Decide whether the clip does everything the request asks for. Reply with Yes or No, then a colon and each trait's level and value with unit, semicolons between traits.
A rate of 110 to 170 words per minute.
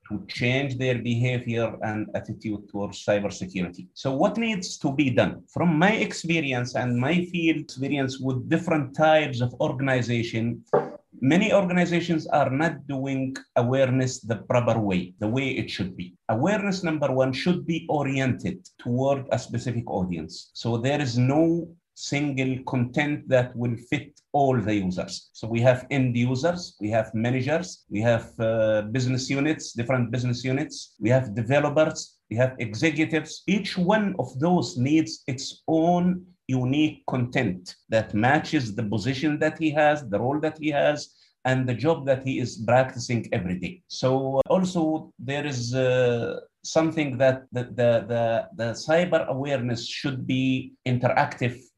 Yes: average, 150 wpm